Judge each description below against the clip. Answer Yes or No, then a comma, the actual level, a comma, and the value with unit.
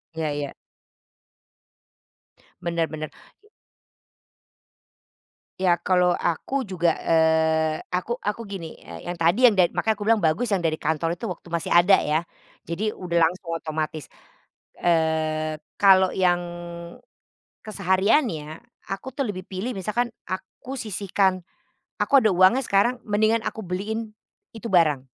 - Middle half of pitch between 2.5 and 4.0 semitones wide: No, average, 4.4 semitones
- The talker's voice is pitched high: No, medium, 180 Hz